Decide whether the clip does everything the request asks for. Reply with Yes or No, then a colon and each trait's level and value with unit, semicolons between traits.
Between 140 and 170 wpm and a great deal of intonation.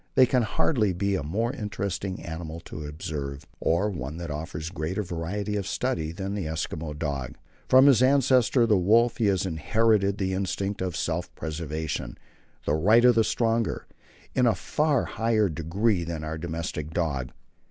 Yes: average, 165 wpm; wide, 5.7 semitones